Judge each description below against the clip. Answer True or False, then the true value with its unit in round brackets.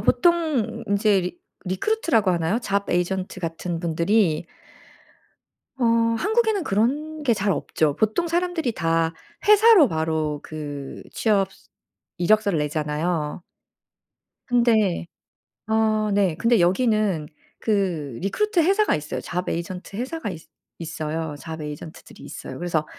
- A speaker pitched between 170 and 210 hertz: True (190 Hz)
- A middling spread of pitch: False (6.3 semitones)